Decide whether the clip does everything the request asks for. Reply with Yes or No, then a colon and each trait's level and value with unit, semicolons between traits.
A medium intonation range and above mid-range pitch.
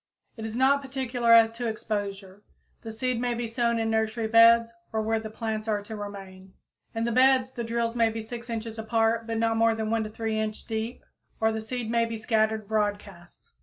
No: narrow, 1.2 semitones; high, 225 Hz